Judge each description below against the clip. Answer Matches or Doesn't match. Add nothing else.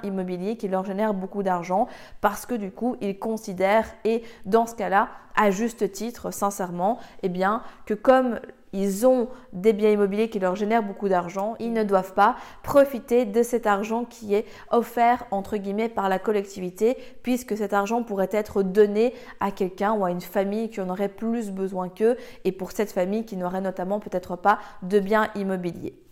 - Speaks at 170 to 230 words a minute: Matches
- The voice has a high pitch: Matches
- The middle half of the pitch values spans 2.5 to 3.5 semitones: Matches